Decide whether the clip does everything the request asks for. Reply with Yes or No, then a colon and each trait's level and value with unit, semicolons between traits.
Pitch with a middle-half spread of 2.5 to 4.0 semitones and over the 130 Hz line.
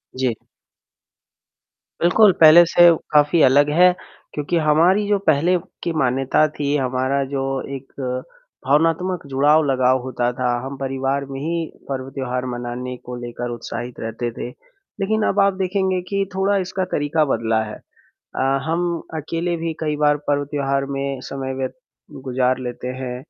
No: average, 4.7 semitones; medium, 140 Hz